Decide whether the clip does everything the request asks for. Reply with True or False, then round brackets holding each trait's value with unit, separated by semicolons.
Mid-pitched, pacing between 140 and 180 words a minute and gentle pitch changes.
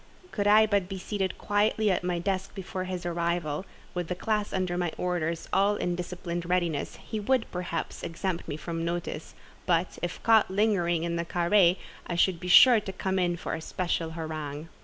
False (180 Hz; 190 wpm; 2.3 semitones)